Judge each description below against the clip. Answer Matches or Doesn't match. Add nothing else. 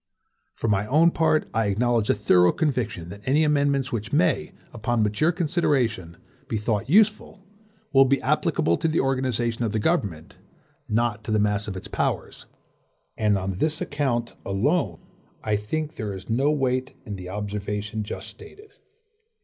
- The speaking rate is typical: Matches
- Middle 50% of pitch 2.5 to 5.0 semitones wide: Doesn't match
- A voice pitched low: Matches